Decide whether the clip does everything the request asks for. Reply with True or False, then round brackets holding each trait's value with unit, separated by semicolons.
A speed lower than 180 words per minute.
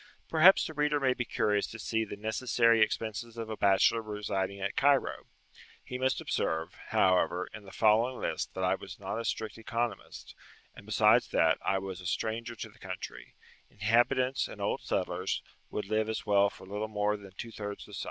False (190 wpm)